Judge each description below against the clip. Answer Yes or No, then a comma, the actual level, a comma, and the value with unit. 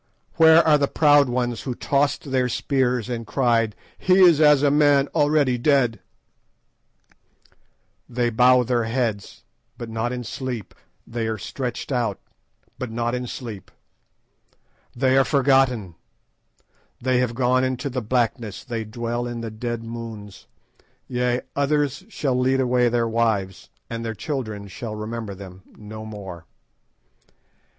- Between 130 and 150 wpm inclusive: Yes, average, 140 wpm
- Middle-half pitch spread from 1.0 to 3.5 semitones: Yes, average, 2.8 semitones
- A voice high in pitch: No, low, 120 Hz